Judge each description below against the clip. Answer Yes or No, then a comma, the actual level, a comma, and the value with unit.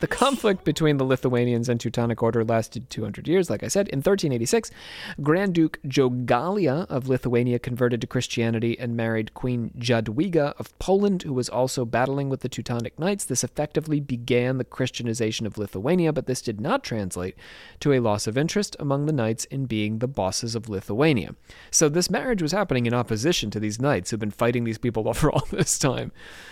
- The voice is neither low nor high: No, low, 125 Hz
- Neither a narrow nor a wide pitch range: Yes, average, 4.5 semitones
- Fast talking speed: No, average, 190 wpm